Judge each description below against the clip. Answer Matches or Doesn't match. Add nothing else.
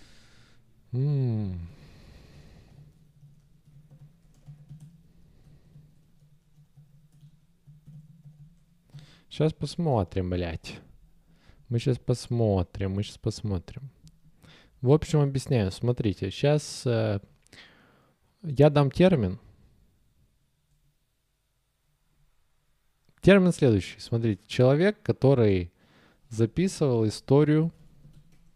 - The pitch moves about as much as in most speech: Matches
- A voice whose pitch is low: Doesn't match